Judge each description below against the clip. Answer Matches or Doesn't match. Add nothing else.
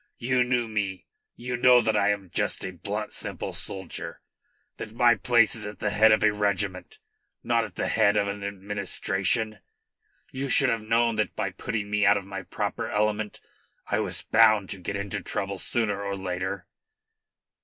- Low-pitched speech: Matches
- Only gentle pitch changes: Matches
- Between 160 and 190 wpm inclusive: Matches